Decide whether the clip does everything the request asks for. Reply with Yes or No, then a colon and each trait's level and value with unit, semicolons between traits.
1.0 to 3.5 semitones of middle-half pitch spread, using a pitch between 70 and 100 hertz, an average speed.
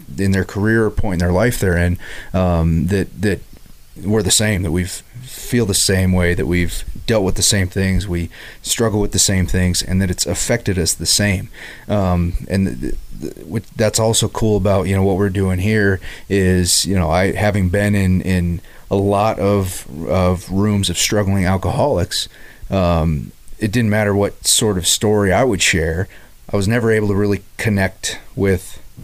Yes: narrow, 2.4 semitones; very low, 95 Hz; average, 190 wpm